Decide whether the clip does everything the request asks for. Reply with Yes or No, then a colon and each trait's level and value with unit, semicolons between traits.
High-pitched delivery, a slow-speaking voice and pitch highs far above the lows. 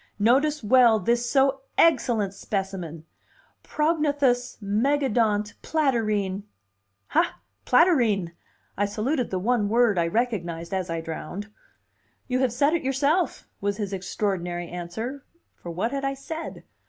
Yes: high, 225 Hz; slow, 125 wpm; wide, 5.7 semitones